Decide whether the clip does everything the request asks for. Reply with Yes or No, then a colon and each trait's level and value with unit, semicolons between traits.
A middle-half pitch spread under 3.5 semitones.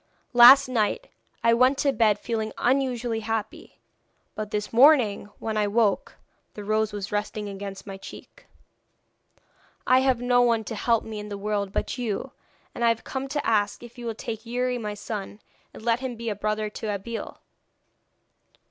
Yes: average, 2.7 semitones